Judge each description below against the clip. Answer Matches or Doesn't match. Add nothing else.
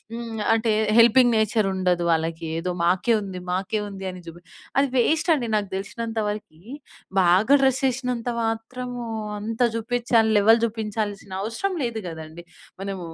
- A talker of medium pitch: Doesn't match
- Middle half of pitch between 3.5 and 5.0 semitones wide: Matches